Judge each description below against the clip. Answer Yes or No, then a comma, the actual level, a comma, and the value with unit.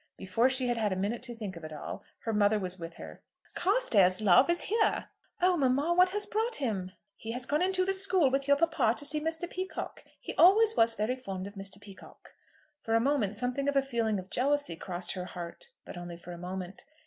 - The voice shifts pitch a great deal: Yes, wide, 8.5 semitones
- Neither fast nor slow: No, fast, 225 wpm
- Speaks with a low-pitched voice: No, high, 240 Hz